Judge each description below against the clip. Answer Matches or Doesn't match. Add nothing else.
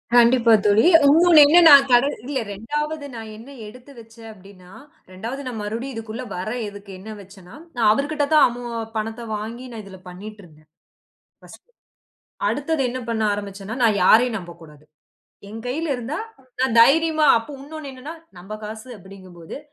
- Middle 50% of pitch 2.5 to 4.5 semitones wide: Doesn't match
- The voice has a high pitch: Matches